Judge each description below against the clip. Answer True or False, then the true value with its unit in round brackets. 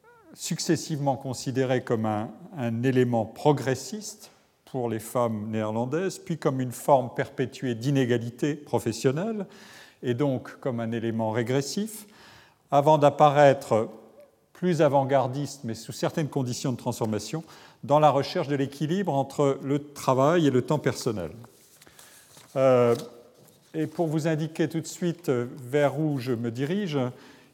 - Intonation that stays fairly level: False (4.3 semitones)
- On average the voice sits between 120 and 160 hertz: True (140 Hz)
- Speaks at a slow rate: True (130 wpm)